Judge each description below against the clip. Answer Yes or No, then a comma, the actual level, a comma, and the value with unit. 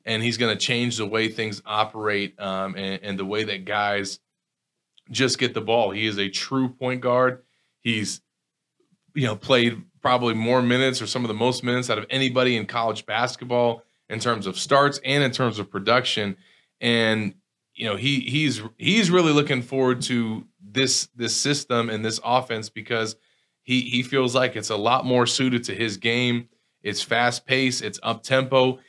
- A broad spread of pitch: No, average, 2.7 semitones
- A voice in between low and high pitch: No, low, 120 Hz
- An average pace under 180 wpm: No, average, 185 wpm